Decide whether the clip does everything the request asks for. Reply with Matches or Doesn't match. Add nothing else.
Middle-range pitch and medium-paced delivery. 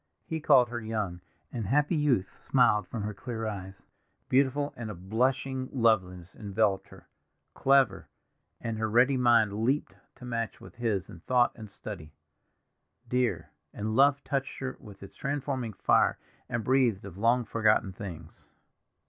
Doesn't match